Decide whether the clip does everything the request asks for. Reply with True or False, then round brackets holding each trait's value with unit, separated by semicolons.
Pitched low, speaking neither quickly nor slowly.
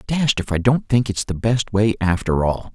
False (105 Hz; 240 wpm)